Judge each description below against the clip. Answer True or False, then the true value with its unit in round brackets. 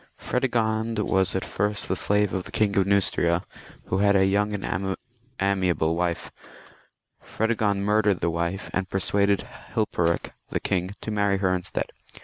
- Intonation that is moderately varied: False (2.0 semitones)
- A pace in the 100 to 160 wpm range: True (155 wpm)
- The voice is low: True (100 Hz)